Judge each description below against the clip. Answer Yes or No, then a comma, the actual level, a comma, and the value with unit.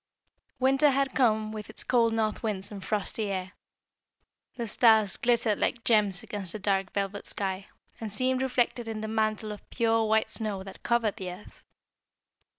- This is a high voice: Yes, high, 215 Hz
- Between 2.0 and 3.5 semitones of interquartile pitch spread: Yes, narrow, 2.5 semitones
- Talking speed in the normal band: Yes, average, 165 wpm